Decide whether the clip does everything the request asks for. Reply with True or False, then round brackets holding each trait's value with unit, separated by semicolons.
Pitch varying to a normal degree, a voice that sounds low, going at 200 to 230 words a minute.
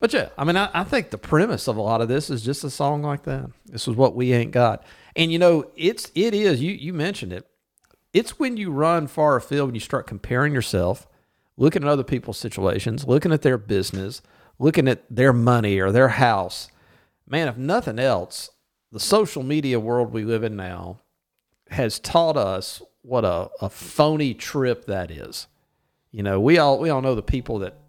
True (4.9 semitones; 130 Hz; 205 wpm)